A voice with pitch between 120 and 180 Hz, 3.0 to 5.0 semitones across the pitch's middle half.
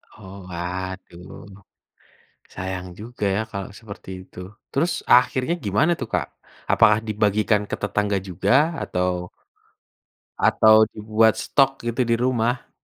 No: low, 105 Hz; average, 3.7 semitones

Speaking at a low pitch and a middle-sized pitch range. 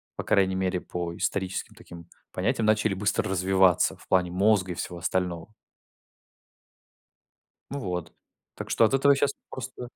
Yes: very low, 95 Hz; average, 3.3 semitones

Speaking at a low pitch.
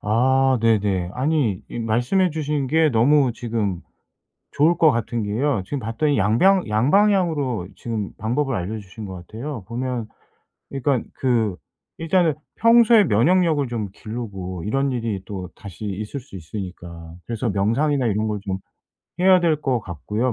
Yes: low, 120 Hz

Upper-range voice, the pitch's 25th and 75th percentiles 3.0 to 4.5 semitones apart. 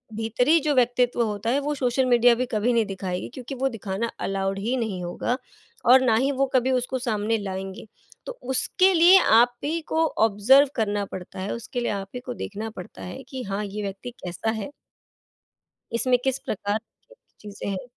Yes: high, 230 Hz; average, 4.2 semitones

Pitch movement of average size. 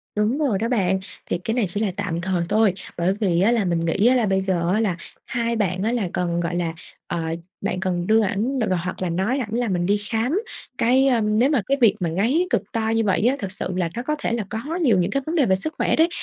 Yes: average, 4.4 semitones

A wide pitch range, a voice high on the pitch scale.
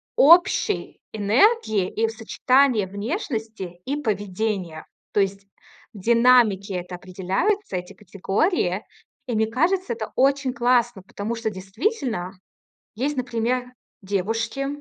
No: average, 4.7 semitones; high, 225 Hz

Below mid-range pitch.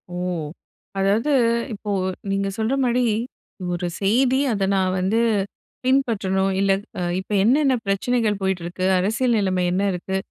No: high, 200 Hz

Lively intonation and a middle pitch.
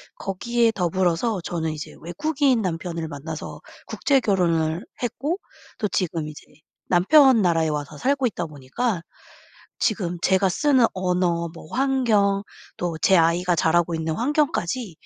Yes: wide, 6.2 semitones; medium, 180 Hz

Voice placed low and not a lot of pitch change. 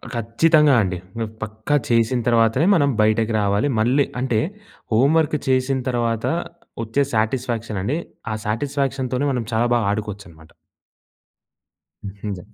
No: low, 115 Hz; average, 3.5 semitones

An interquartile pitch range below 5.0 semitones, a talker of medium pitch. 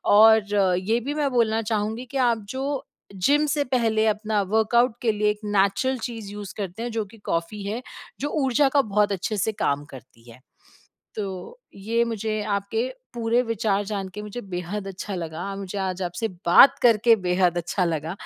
No: average, 3.1 semitones; high, 210 Hz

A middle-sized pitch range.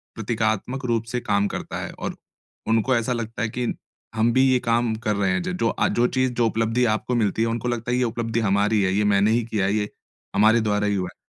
No: narrow, 2.3 semitones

